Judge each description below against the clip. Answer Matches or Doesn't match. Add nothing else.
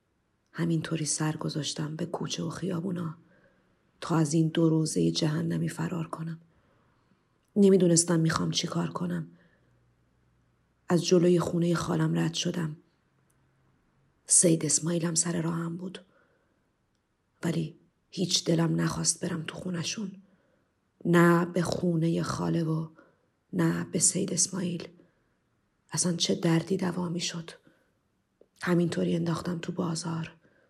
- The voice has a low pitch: Doesn't match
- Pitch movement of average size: Doesn't match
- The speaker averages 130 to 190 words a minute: Doesn't match